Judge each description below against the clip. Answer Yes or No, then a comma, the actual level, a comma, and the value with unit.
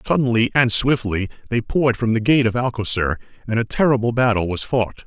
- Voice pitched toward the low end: Yes, low, 115 Hz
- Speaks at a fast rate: No, average, 190 wpm